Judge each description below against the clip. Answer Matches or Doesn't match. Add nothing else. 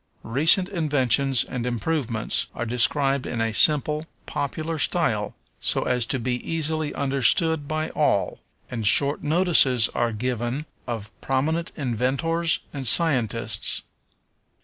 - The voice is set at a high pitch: Doesn't match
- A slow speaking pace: Matches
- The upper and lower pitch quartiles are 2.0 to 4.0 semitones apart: Doesn't match